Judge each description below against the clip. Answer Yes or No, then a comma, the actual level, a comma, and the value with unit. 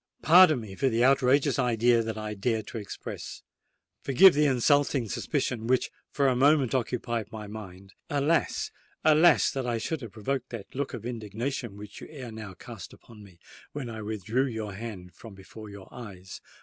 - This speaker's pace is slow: No, average, 175 wpm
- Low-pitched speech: Yes, low, 115 Hz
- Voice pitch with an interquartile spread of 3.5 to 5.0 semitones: Yes, average, 4.1 semitones